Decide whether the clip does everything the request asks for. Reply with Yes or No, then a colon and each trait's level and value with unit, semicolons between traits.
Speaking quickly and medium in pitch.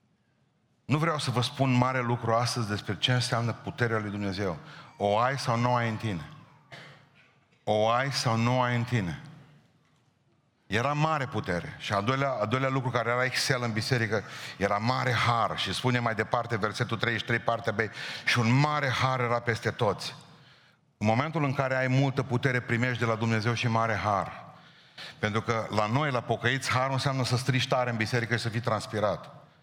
No: fast, 185 wpm; low, 120 Hz